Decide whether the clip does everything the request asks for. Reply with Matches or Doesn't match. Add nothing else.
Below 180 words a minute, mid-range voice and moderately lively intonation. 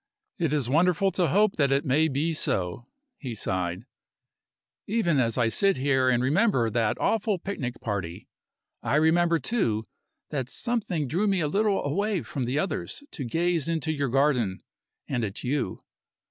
Doesn't match